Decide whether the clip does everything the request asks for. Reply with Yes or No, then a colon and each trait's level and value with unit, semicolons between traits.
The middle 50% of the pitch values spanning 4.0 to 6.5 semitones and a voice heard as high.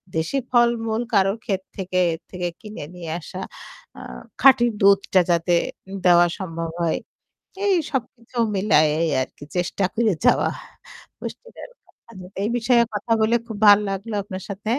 Yes: average, 4.5 semitones; high, 200 Hz